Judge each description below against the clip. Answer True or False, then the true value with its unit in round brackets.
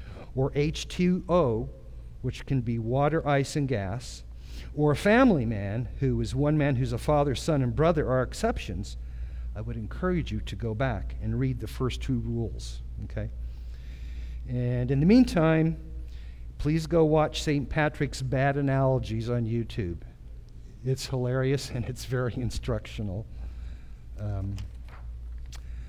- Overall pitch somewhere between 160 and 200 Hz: False (120 Hz)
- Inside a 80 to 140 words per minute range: True (135 wpm)